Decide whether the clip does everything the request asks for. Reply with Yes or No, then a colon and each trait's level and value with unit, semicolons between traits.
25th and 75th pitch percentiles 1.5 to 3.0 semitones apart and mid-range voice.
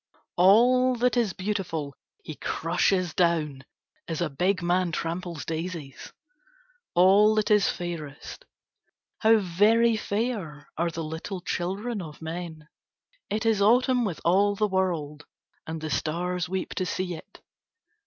No: average, 4.4 semitones; medium, 180 Hz